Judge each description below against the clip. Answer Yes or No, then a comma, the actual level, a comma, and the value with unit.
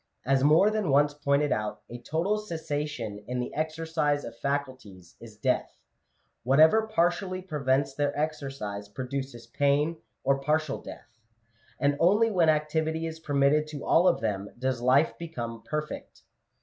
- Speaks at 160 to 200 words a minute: No, average, 145 wpm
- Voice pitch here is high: No, medium, 145 Hz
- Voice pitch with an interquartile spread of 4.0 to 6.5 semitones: No, average, 3.5 semitones